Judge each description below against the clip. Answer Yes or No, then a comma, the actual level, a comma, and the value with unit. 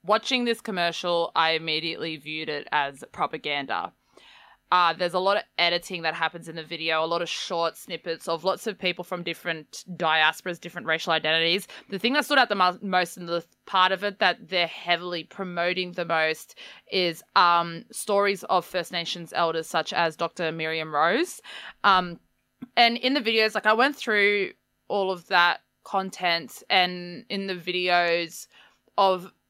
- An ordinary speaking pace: Yes, average, 175 wpm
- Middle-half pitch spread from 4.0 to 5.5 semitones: No, average, 2.8 semitones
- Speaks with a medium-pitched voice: Yes, medium, 175 Hz